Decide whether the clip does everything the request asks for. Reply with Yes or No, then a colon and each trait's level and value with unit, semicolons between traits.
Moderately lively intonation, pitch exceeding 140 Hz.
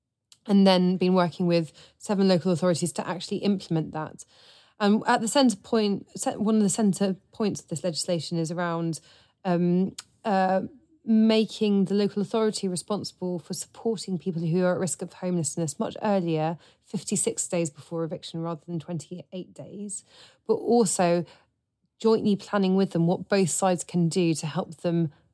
Yes: average, 3.2 semitones; medium, 185 Hz